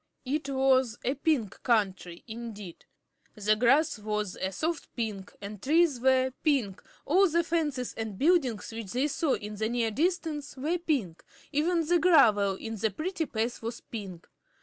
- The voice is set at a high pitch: Yes, very high, 250 Hz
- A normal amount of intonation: No, wide, 6.4 semitones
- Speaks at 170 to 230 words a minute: No, average, 160 wpm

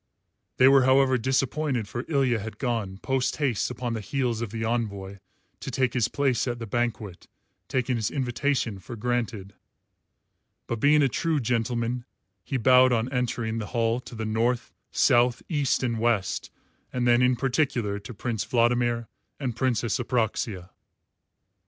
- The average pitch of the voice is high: No, low, 120 Hz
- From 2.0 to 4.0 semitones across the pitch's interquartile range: Yes, narrow, 2.4 semitones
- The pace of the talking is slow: No, average, 155 wpm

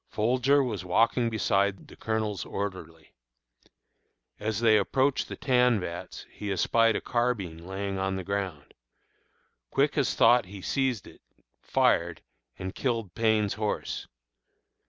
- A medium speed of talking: No, slow, 130 wpm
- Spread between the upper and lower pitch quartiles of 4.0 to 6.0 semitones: No, average, 3.6 semitones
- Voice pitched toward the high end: No, low, 105 Hz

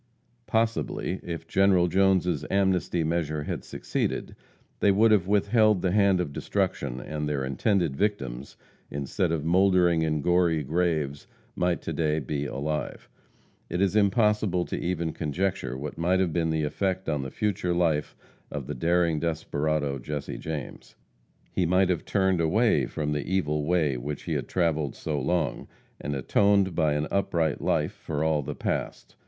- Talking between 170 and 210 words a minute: No, average, 160 wpm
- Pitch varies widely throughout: No, average, 4.1 semitones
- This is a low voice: Yes, very low, 85 Hz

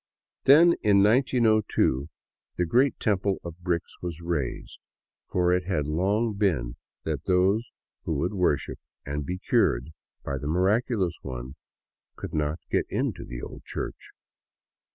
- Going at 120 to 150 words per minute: Yes, slow, 135 wpm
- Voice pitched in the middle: No, very low, 90 Hz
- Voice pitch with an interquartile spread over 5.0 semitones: Yes, wide, 5.6 semitones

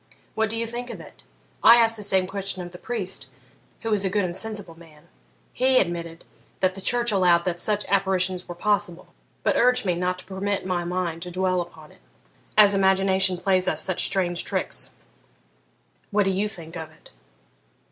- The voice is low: No, high, 190 Hz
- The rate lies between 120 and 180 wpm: No, average, 190 wpm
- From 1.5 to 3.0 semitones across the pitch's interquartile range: Yes, average, 2.7 semitones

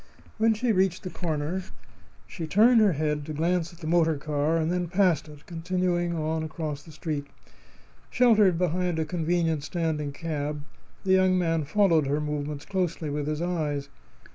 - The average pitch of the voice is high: No, medium, 165 Hz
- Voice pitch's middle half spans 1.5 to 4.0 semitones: Yes, average, 3.1 semitones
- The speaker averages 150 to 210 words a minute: Yes, average, 165 wpm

